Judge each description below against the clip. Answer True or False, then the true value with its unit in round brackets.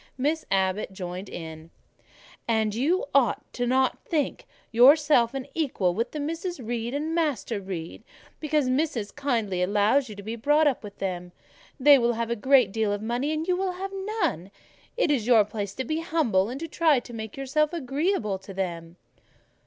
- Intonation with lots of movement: True (6.7 semitones)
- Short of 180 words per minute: False (185 wpm)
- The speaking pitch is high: True (245 Hz)